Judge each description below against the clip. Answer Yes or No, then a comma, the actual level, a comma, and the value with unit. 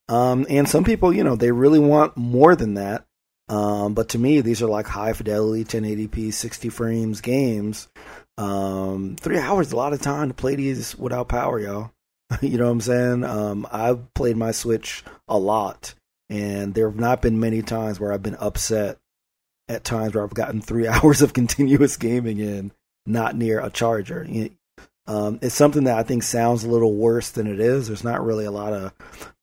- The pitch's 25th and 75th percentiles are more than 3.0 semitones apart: No, average, 2.7 semitones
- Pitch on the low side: Yes, low, 115 Hz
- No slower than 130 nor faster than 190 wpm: No, average, 200 wpm